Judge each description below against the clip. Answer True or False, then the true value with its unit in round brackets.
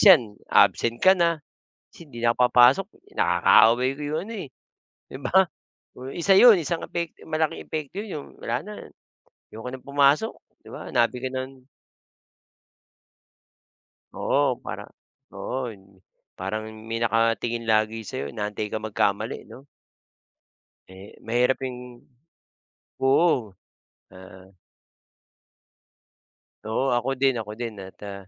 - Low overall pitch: True (125 Hz)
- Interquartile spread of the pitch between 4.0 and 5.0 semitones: True (4.7 semitones)